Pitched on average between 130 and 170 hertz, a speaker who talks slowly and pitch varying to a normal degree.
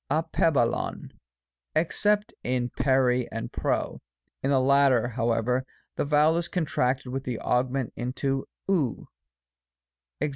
Yes: low, 135 Hz; slow, 115 wpm; average, 3.1 semitones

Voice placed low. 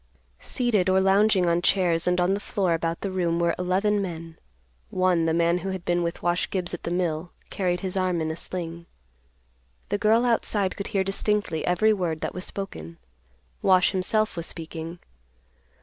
No: medium, 180 Hz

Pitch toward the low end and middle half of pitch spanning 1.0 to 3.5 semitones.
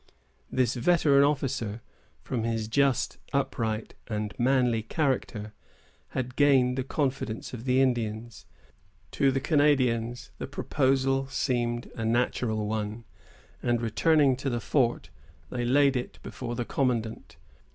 Yes: low, 125 Hz; average, 2.8 semitones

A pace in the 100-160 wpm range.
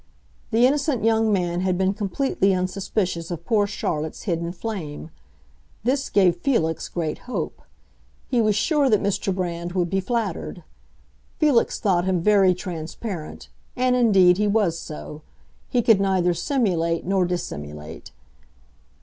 Yes: slow, 135 wpm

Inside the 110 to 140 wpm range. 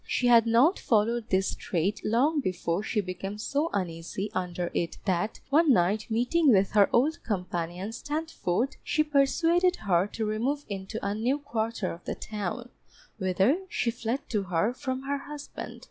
No: average, 160 wpm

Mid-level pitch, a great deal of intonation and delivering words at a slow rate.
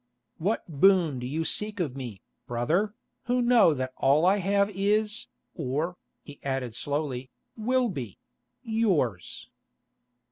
Yes: medium, 160 Hz; wide, 8.2 semitones; slow, 120 wpm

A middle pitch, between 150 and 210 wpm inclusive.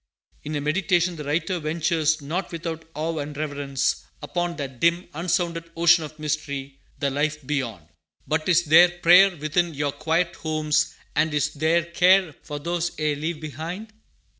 Yes: medium, 160 Hz; average, 160 wpm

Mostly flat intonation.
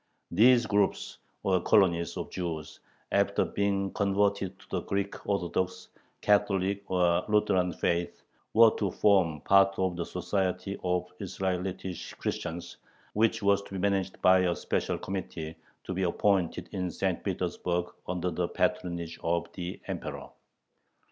Yes: narrow, 2.1 semitones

